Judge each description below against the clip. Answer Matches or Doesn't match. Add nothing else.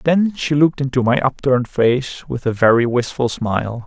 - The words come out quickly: Doesn't match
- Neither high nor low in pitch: Doesn't match